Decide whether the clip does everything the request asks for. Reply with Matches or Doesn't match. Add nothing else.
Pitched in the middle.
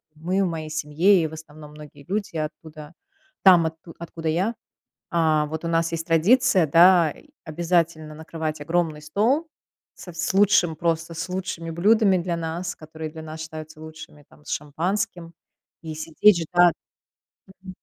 Matches